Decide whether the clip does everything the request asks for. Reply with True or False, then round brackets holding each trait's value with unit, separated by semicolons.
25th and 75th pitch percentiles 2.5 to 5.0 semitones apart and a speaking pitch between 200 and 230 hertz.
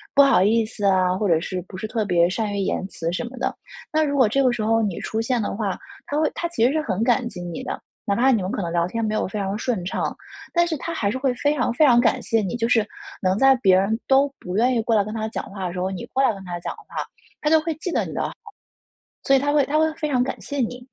False (5.5 semitones; 225 Hz)